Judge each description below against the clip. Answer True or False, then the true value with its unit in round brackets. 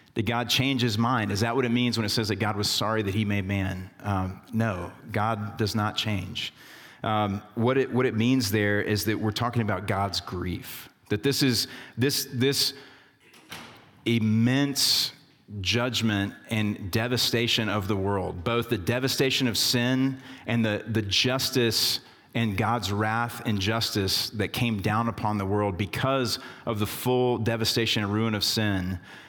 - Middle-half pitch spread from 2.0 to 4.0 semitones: True (2.9 semitones)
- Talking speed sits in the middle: True (170 wpm)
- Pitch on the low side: True (115 Hz)